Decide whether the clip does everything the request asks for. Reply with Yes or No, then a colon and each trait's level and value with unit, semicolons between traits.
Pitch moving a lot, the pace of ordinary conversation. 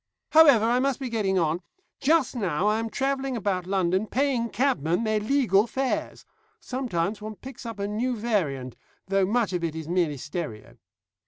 Yes: wide, 5.8 semitones; average, 170 wpm